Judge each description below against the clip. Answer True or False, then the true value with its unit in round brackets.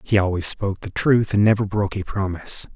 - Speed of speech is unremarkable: False (215 wpm)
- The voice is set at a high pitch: False (100 Hz)